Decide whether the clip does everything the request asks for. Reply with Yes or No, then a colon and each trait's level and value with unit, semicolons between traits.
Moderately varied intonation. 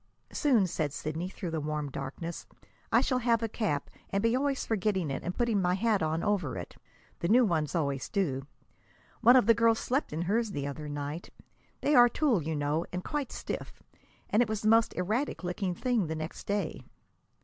No: wide, 6.7 semitones